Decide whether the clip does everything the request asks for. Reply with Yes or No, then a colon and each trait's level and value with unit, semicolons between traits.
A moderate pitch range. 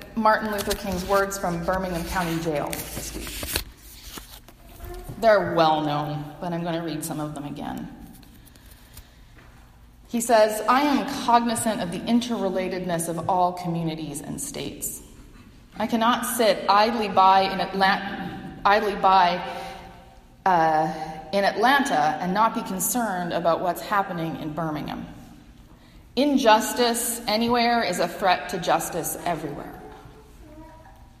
Yes: average, 5.0 semitones